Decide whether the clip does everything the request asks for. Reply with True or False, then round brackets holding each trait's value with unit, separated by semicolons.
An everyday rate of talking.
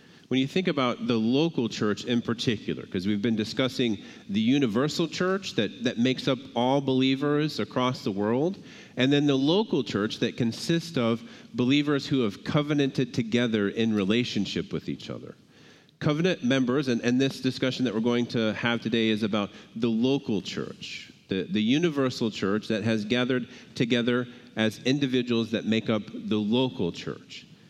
True (165 wpm)